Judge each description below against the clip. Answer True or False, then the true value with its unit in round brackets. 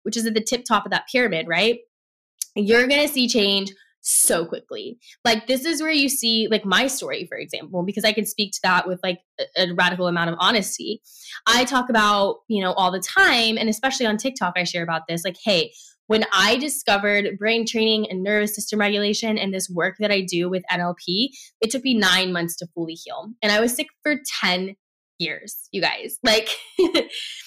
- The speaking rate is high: True (210 wpm)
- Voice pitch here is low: False (215 Hz)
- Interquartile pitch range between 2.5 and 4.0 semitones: False (4.9 semitones)